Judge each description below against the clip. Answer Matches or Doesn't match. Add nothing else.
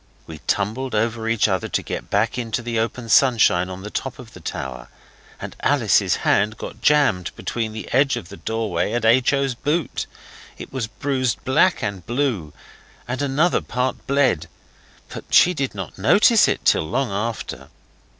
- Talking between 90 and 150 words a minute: Doesn't match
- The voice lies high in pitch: Doesn't match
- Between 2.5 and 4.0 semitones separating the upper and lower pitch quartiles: Doesn't match